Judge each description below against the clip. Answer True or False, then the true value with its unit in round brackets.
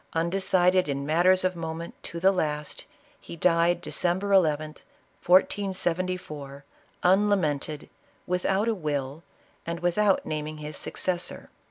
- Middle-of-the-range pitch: True (170 Hz)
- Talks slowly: True (115 wpm)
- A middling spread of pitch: True (3.3 semitones)